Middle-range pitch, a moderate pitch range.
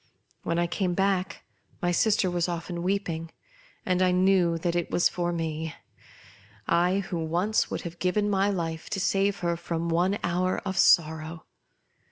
No: medium, 175 Hz; narrow, 2.2 semitones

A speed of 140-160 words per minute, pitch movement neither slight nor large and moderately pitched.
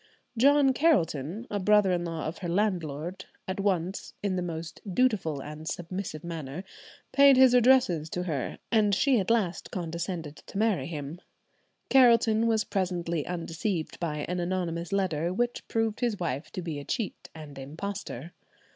Yes: average, 155 wpm; average, 4.8 semitones; medium, 180 Hz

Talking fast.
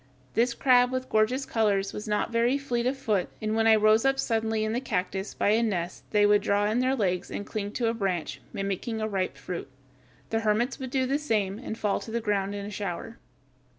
Yes: fast, 220 wpm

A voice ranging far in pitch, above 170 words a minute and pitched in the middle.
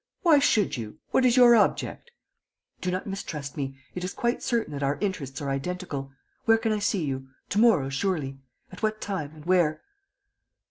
Yes: wide, 7.5 semitones; average, 185 wpm; medium, 180 Hz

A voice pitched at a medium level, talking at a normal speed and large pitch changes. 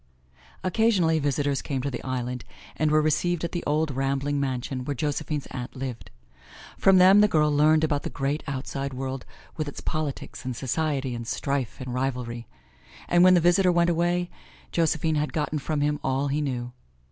No: medium, 145 Hz; average, 180 wpm; average, 3.2 semitones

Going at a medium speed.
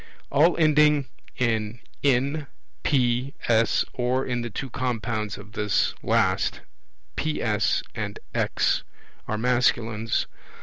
No: slow, 105 wpm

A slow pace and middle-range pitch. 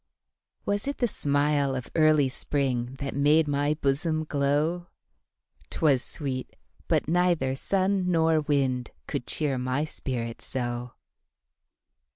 Yes: slow, 105 wpm; medium, 145 Hz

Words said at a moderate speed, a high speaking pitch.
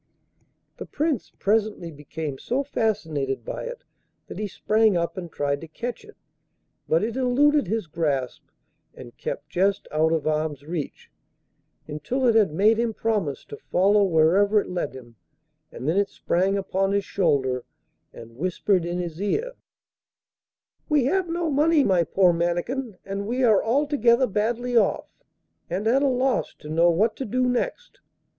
Yes: average, 160 wpm; high, 200 Hz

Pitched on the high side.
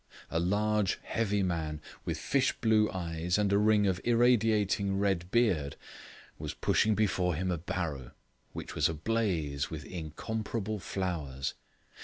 No: very low, 95 Hz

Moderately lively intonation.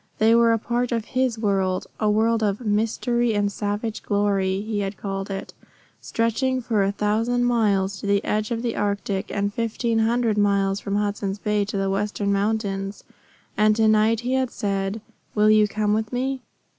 No: narrow, 2.2 semitones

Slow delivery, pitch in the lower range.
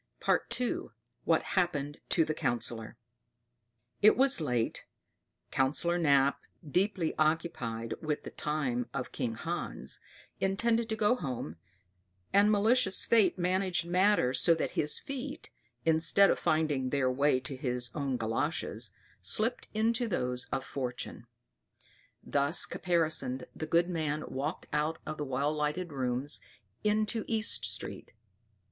No: slow, 125 wpm; medium, 155 Hz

